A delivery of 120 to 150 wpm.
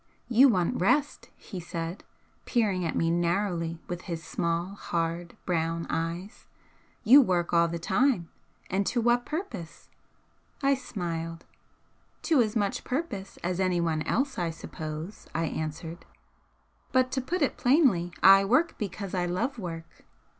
Yes: average, 140 wpm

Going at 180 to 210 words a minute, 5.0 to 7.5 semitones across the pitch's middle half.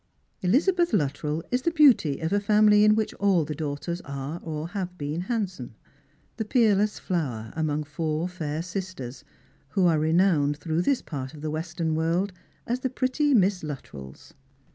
No: average, 165 wpm; wide, 5.4 semitones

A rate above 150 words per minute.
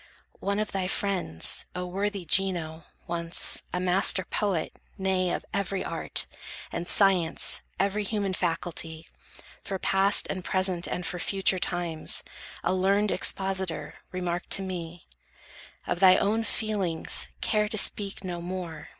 No: slow, 135 wpm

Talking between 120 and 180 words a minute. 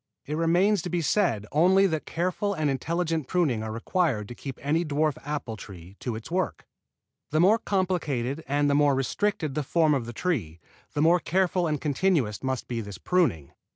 No: average, 190 wpm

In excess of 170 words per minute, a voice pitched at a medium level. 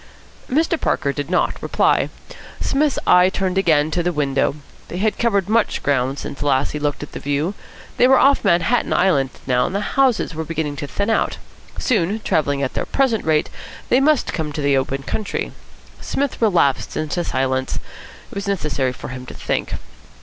Yes: average, 185 wpm; medium, 165 Hz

